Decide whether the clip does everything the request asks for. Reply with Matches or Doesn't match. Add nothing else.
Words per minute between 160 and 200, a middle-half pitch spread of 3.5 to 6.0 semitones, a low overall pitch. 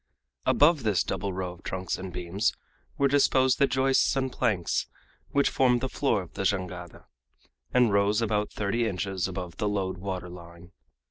Matches